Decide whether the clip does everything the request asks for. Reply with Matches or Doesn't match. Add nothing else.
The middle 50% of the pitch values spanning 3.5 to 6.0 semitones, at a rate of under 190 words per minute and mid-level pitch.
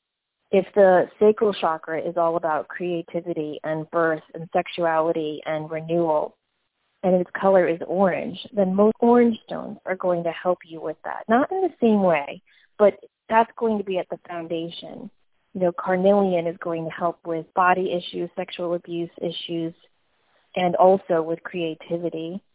Doesn't match